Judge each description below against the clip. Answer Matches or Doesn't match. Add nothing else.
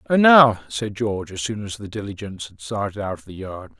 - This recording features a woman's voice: Doesn't match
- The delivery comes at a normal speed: Doesn't match